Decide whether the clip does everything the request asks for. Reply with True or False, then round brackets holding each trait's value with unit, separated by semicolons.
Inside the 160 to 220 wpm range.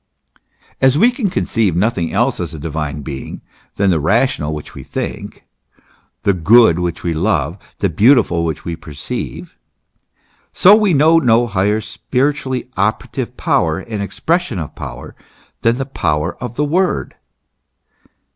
False (145 wpm)